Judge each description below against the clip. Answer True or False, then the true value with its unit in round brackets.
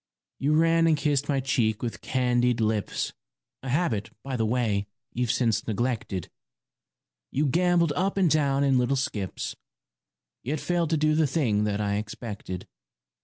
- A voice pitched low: True (130 Hz)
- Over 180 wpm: False (155 wpm)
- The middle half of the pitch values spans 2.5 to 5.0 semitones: False (5.6 semitones)